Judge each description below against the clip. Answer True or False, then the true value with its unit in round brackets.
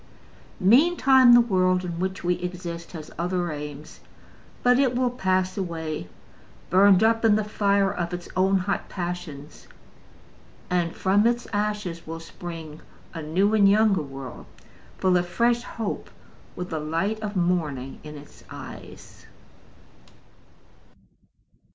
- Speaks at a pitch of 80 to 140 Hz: False (185 Hz)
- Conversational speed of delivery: False (130 wpm)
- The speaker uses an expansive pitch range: False (3.9 semitones)